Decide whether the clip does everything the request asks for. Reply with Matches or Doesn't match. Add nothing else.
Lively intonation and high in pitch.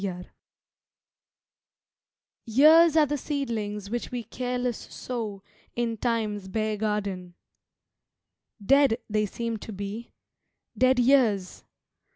Doesn't match